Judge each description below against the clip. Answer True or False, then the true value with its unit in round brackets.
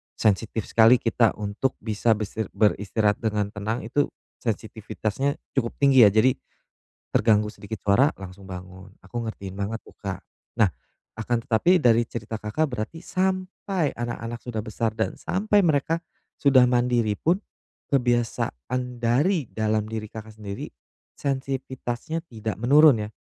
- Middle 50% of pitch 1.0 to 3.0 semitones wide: False (3.7 semitones)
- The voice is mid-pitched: False (115 Hz)